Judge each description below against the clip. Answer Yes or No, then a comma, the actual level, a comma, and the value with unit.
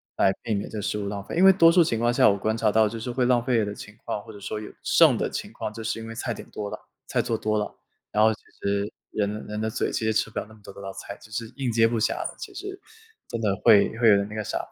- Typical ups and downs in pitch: No, narrow, 1.8 semitones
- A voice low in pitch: Yes, low, 110 Hz